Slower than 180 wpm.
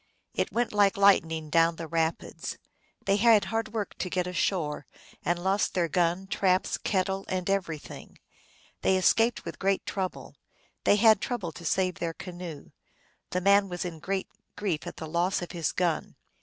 Yes: average, 170 wpm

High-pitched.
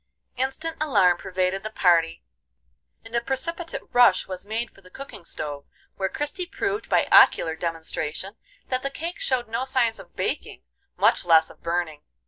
Yes: high, 215 Hz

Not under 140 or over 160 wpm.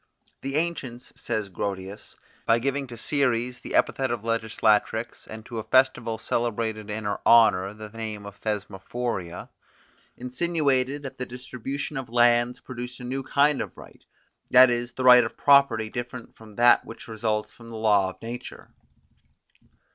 Yes: average, 155 wpm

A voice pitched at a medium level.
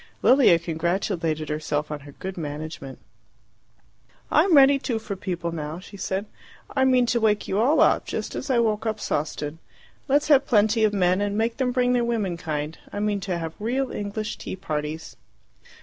No: high, 200 Hz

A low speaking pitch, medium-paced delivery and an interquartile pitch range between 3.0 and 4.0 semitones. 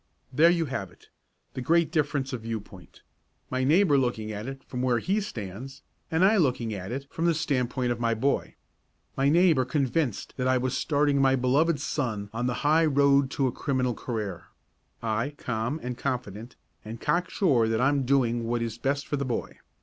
Yes: low, 130 Hz; average, 190 wpm; average, 3.7 semitones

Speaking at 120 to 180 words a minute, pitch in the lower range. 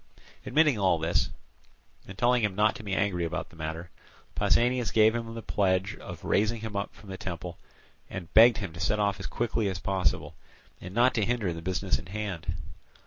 No: average, 195 wpm; low, 100 Hz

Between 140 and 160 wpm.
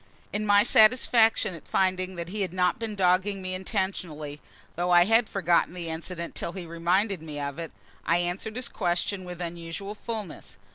No: average, 180 wpm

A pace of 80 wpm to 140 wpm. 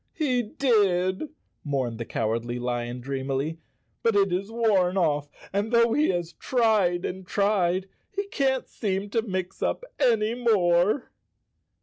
Yes: slow, 135 wpm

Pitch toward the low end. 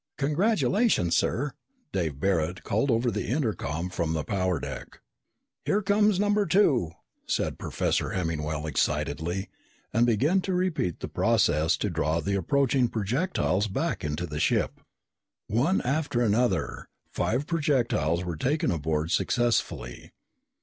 Yes: low, 110 Hz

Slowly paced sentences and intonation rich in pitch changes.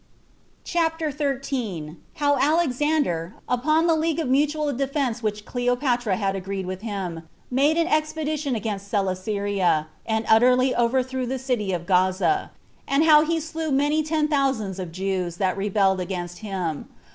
No: average, 145 wpm; wide, 7.4 semitones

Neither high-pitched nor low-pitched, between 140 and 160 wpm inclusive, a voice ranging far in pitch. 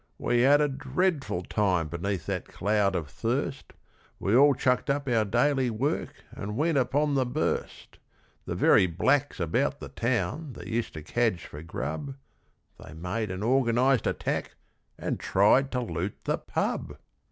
No: low, 120 Hz; average, 155 wpm; wide, 6.2 semitones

